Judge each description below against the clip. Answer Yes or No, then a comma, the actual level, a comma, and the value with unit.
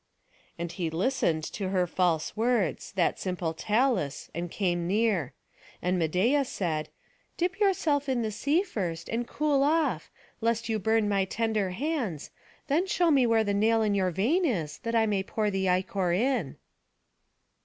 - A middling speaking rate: Yes, average, 165 wpm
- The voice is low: No, high, 210 Hz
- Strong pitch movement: Yes, wide, 5.9 semitones